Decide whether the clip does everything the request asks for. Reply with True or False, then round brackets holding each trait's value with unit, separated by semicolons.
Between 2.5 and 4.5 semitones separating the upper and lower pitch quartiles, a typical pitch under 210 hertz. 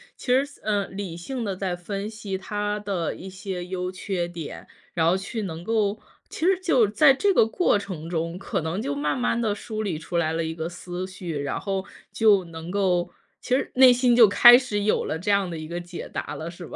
True (3.9 semitones; 190 Hz)